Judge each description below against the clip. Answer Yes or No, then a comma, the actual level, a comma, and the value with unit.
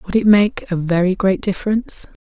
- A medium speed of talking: Yes, average, 190 wpm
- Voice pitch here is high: Yes, high, 195 Hz